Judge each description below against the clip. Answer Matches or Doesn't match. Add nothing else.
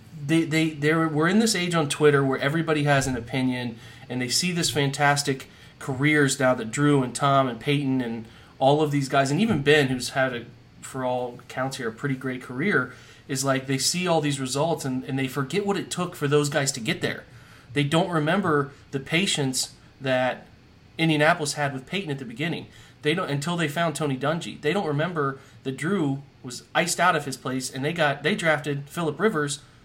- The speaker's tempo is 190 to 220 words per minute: Matches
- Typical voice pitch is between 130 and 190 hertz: Matches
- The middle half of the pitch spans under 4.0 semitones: Matches